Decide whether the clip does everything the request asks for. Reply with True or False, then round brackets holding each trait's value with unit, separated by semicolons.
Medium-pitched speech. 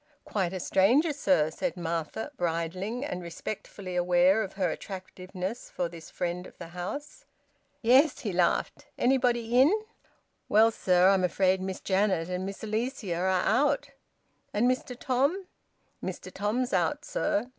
False (195 Hz)